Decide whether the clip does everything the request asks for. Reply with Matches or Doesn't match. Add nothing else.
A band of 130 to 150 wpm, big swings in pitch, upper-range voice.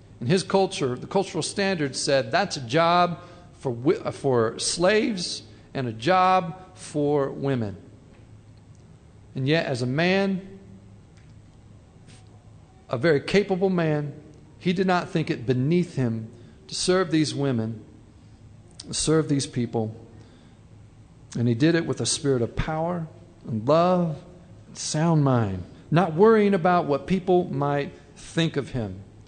Doesn't match